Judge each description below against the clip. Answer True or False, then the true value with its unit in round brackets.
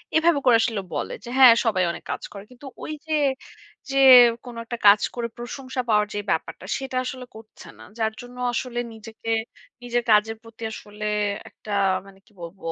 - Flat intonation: False (3.1 semitones)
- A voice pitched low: False (230 Hz)